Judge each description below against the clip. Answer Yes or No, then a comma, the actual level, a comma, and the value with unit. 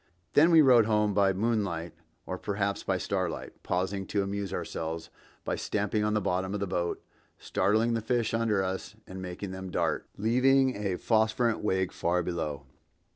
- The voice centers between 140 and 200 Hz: No, low, 100 Hz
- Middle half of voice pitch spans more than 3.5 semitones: No, average, 2.9 semitones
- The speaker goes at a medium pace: Yes, average, 170 wpm